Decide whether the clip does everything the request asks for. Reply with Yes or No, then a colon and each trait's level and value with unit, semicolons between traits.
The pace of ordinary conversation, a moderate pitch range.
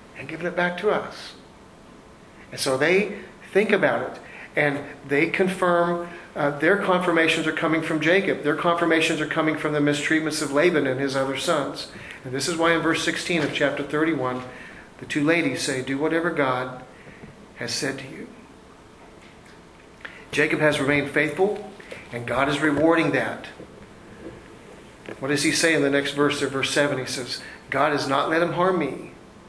Yes: average, 175 wpm; average, 3.3 semitones